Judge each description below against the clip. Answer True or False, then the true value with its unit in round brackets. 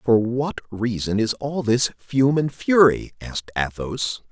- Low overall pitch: True (120 Hz)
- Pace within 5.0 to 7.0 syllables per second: False (3.8 syllables/s)